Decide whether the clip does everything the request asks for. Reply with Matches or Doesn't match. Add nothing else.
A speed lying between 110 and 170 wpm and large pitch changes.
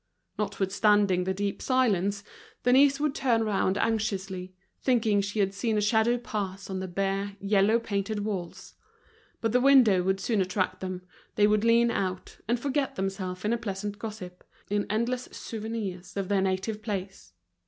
Doesn't match